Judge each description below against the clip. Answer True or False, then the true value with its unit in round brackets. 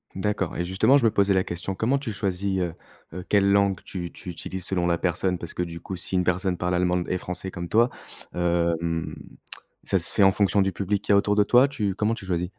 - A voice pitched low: True (95 Hz)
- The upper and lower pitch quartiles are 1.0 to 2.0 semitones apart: False (2.4 semitones)